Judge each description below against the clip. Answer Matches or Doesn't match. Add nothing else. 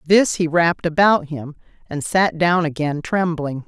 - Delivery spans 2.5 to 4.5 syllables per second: Matches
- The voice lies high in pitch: Doesn't match